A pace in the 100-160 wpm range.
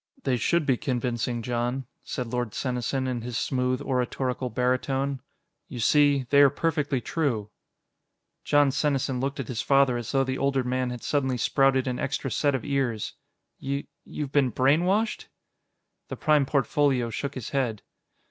Yes: average, 155 wpm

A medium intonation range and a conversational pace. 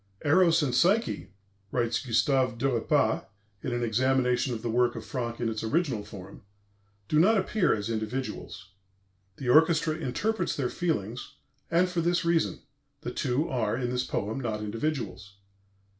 No: wide, 5.9 semitones; average, 150 wpm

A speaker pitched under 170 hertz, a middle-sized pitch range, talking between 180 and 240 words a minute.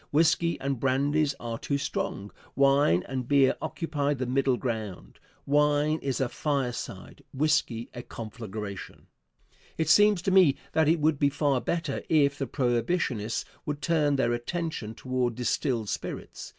No: medium, 140 Hz; average, 3.8 semitones; average, 145 wpm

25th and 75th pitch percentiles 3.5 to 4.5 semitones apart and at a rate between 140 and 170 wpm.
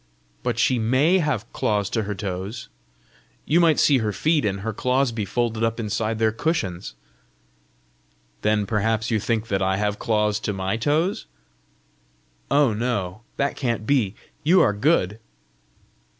Yes: average, 3.8 semitones; average, 150 wpm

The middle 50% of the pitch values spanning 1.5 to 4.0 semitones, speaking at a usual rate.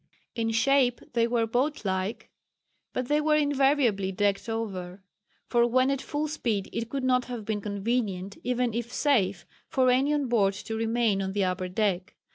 No: average, 4.4 semitones; average, 175 wpm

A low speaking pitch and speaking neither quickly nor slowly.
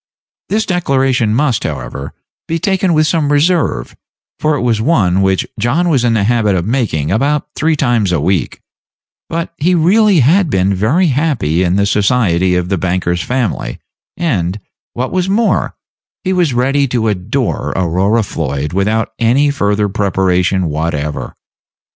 Yes: low, 115 Hz; average, 155 wpm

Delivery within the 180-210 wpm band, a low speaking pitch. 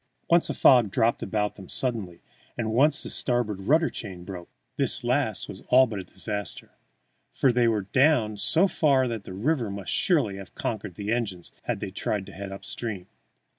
Yes: average, 190 wpm; low, 110 Hz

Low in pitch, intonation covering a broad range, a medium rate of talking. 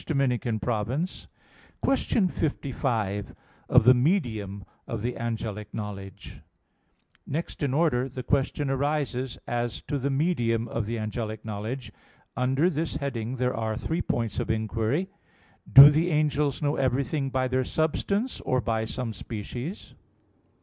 No: low, 125 Hz; average, 4.4 semitones; average, 145 wpm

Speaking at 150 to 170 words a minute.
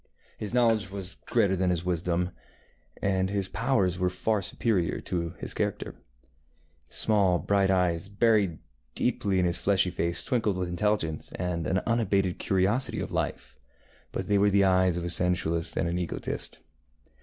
Yes: average, 160 wpm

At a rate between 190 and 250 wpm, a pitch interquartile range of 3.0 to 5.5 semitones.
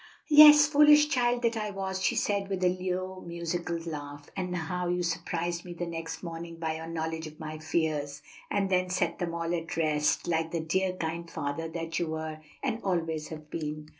No: average, 195 wpm; narrow, 2.5 semitones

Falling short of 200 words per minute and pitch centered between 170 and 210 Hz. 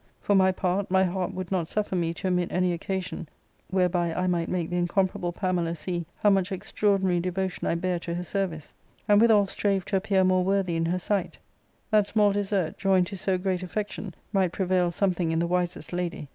No: fast, 205 wpm; medium, 185 Hz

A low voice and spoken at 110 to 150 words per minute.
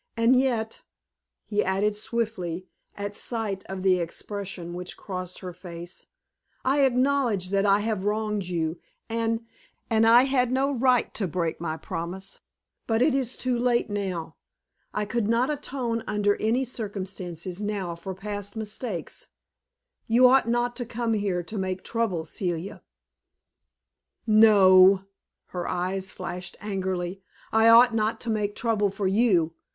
No: high, 205 Hz; average, 145 wpm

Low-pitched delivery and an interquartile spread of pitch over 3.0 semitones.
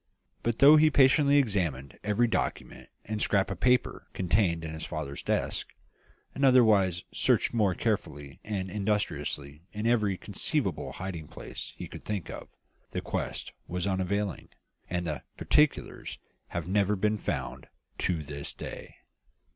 Yes: low, 100 Hz; average, 4.6 semitones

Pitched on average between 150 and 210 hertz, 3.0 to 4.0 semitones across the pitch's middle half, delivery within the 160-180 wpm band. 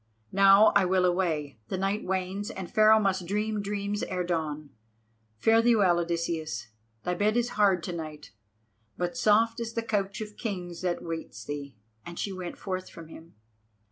Yes: medium, 185 Hz; average, 3.7 semitones; average, 170 wpm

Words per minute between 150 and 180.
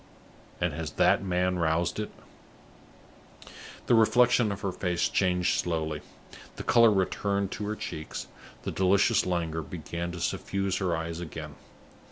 No: average, 140 wpm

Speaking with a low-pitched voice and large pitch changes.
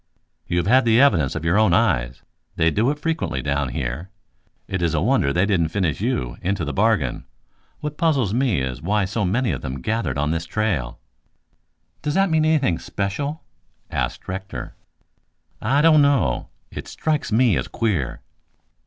Yes: low, 100 Hz; wide, 8.6 semitones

